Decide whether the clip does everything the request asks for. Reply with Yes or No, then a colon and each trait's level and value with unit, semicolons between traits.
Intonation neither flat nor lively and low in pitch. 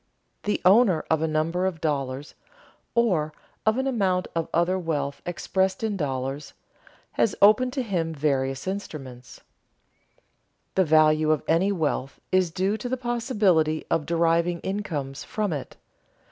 No: average, 4.6 semitones; medium, 170 Hz